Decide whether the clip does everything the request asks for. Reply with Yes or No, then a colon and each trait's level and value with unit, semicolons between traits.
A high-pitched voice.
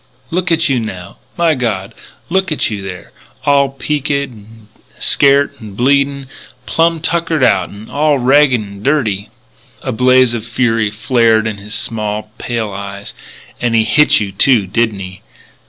No: low, 120 Hz